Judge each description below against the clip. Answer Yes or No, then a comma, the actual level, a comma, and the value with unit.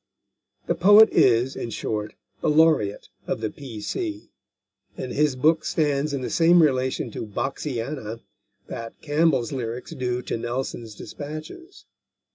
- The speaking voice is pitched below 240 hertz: Yes, low, 135 Hz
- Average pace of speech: No, slow, 130 wpm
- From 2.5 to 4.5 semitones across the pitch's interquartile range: No, average, 4.9 semitones